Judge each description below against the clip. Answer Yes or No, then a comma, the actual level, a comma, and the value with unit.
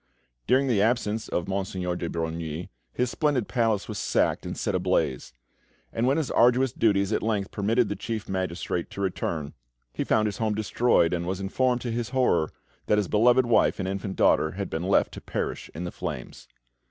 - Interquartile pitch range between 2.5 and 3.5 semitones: No, average, 4.8 semitones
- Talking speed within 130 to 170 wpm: No, average, 190 wpm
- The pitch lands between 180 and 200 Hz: No, low, 105 Hz